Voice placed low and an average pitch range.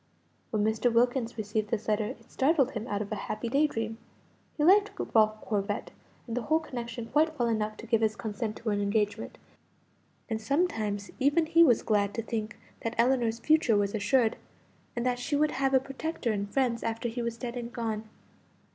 No: high, 230 Hz; average, 3.4 semitones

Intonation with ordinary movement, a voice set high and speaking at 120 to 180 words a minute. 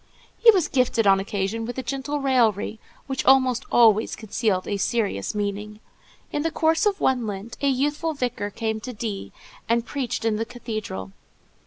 Yes: average, 4.1 semitones; high, 230 Hz; average, 170 wpm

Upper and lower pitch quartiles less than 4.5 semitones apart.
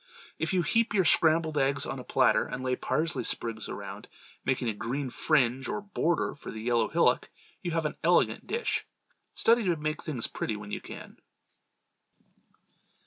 No: average, 5.1 semitones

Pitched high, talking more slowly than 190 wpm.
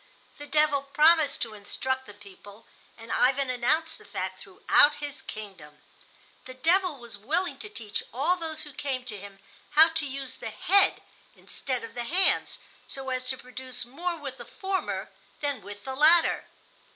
Yes: very high, 270 Hz; average, 170 wpm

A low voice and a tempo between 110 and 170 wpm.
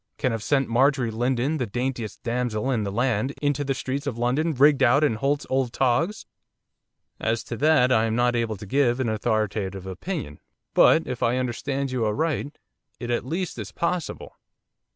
No: low, 125 Hz; average, 180 wpm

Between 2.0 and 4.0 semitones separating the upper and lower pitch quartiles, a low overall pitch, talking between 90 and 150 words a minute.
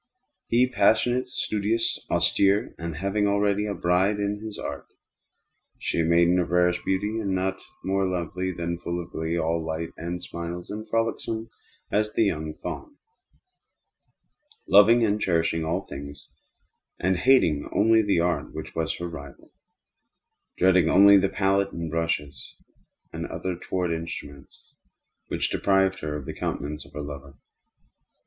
Yes: average, 3.7 semitones; very low, 90 Hz; average, 145 wpm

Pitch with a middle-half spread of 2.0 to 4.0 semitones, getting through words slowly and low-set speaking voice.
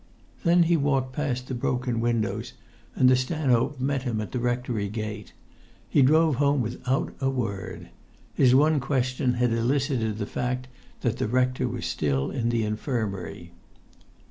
No: average, 2.8 semitones; average, 155 wpm; low, 125 Hz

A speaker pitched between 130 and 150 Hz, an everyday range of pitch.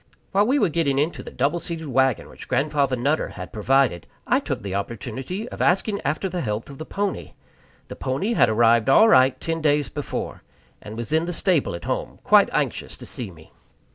No: medium, 140 Hz; wide, 6.2 semitones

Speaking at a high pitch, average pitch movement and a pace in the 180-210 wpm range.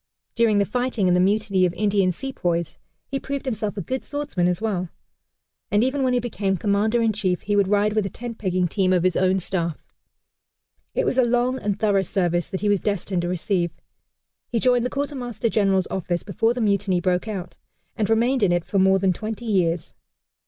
Yes: high, 205 Hz; average, 3.9 semitones; fast, 205 wpm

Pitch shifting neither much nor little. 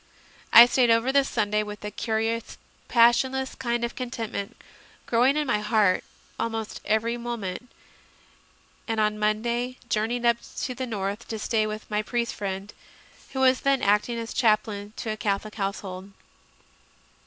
No: narrow, 2.3 semitones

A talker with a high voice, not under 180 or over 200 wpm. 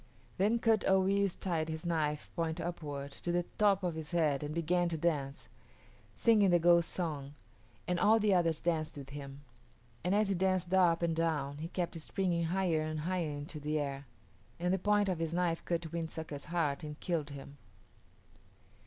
No: medium, 170 Hz; average, 190 wpm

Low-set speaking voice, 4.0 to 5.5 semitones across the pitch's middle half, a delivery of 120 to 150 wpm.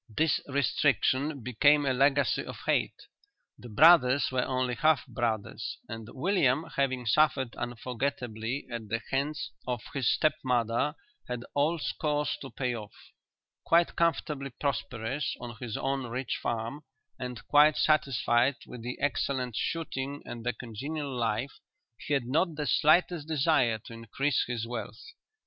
No: low, 130 Hz; average, 3.6 semitones; average, 140 wpm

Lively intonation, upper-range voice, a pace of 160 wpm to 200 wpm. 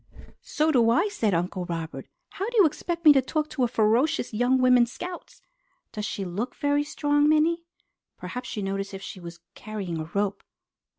Yes: wide, 7.4 semitones; high, 245 Hz; average, 180 wpm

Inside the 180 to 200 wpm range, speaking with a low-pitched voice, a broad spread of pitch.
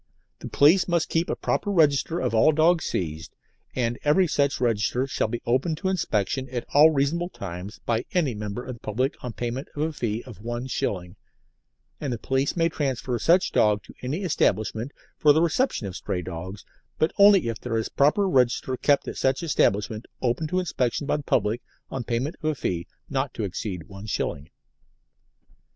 Yes: average, 190 wpm; low, 130 Hz; wide, 6.1 semitones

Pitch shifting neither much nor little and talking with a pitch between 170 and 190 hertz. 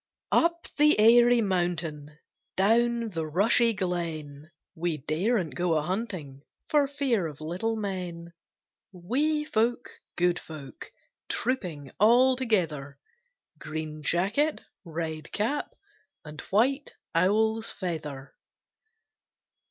No: wide, 6.8 semitones; medium, 185 Hz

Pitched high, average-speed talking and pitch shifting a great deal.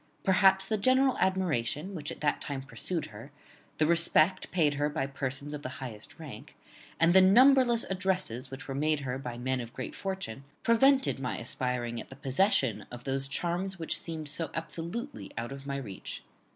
No: medium, 150 Hz; average, 180 wpm; wide, 6.2 semitones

